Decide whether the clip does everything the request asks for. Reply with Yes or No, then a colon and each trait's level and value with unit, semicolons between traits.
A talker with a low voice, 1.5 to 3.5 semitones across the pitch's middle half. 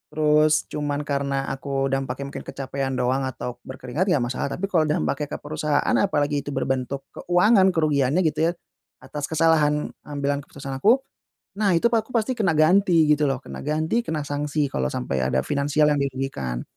No: medium, 145 Hz; average, 2.8 semitones